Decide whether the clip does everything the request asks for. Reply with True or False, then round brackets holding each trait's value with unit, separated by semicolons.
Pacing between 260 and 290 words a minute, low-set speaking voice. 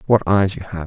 True (280 wpm; 95 Hz)